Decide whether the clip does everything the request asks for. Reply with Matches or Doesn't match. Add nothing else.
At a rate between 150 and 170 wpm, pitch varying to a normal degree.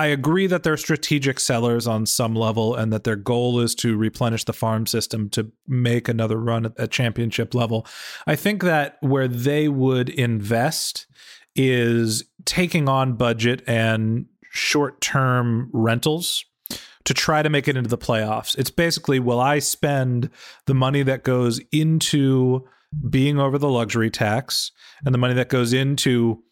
Matches